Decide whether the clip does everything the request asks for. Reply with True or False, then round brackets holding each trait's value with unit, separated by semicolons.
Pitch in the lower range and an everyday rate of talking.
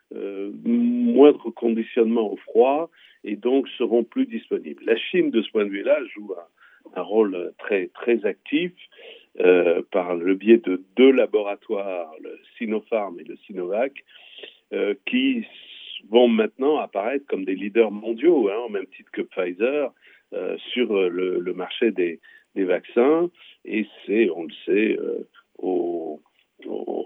False (300 Hz; 150 wpm)